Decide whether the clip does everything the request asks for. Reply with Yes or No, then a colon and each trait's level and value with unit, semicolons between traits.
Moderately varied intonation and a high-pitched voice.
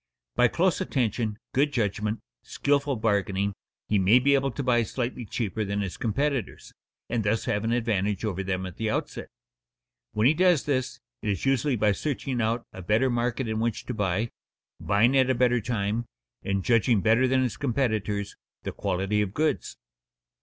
No: average, 3.9 semitones; low, 115 Hz